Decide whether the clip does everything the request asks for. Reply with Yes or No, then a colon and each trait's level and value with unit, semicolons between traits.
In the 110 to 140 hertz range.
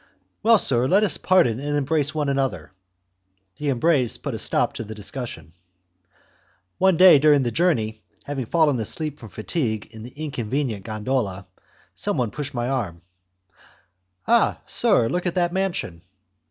Yes: low, 135 Hz